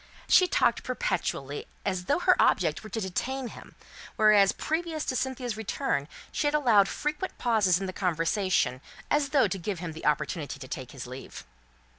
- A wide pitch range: Yes, wide, 7.7 semitones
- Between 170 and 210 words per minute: Yes, average, 175 wpm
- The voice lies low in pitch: No, high, 205 Hz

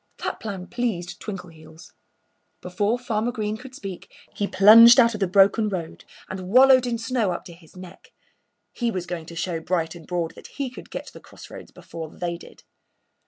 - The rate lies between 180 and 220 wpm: Yes, average, 190 wpm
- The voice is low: No, high, 195 Hz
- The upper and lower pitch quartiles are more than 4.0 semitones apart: Yes, average, 4.8 semitones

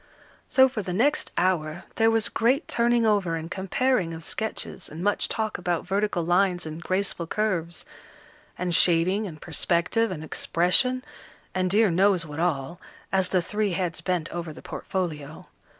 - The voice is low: No, medium, 185 Hz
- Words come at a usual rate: Yes, average, 160 wpm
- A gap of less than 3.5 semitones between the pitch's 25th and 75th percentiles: No, average, 4.0 semitones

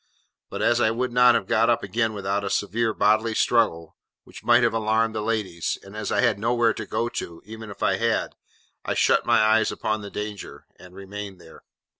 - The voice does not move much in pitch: Yes, narrow, 2.2 semitones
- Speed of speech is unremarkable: No, fast, 210 wpm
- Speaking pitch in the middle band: No, low, 110 Hz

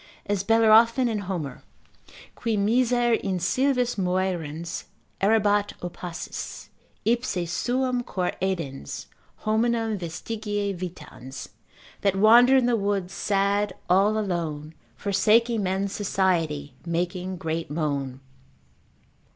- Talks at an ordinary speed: No, slow, 100 wpm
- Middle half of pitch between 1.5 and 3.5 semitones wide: No, average, 4.4 semitones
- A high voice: Yes, high, 195 Hz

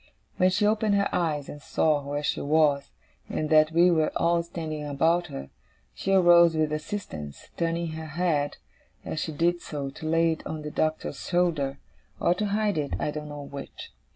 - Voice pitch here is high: No, medium, 160 Hz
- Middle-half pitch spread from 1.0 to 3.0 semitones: Yes, average, 2.7 semitones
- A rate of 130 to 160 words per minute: No, average, 185 wpm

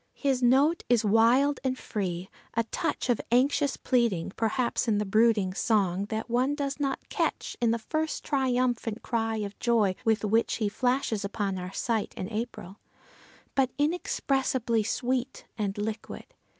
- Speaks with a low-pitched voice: No, high, 230 Hz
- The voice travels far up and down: No, average, 3.6 semitones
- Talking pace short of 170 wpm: Yes, average, 150 wpm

